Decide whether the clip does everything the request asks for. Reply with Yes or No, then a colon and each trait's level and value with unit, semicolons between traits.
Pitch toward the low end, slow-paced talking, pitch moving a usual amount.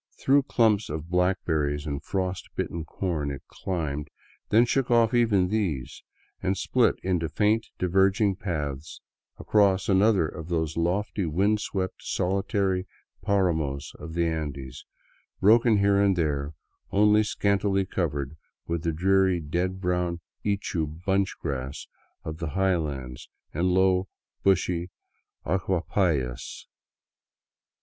Yes: very low, 90 Hz; slow, 120 wpm; average, 3.9 semitones